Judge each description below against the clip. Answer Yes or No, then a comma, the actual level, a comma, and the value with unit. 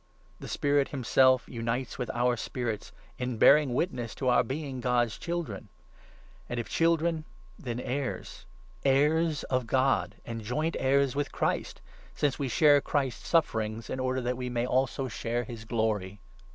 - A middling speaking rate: Yes, average, 165 wpm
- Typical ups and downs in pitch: Yes, average, 3.0 semitones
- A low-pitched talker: Yes, low, 130 Hz